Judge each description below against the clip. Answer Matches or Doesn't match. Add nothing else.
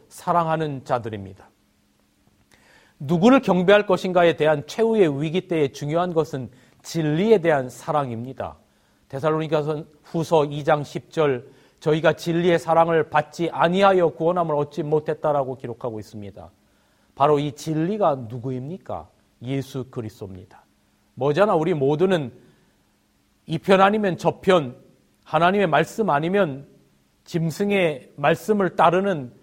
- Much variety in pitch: Doesn't match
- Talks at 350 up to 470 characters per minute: Doesn't match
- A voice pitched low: Doesn't match